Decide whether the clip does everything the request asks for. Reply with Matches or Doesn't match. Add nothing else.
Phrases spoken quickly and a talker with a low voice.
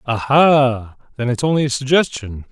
Doesn't match